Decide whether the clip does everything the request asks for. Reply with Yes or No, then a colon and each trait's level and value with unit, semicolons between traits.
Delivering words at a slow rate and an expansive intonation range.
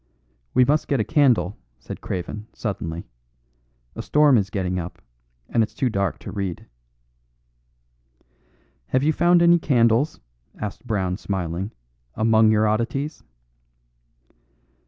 Yes: slow, 120 wpm; wide, 5.7 semitones